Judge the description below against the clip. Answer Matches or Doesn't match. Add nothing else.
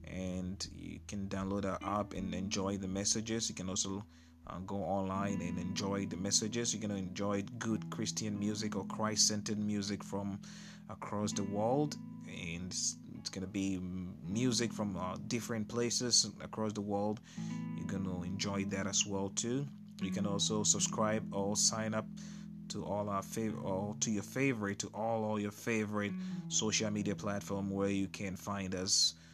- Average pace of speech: Doesn't match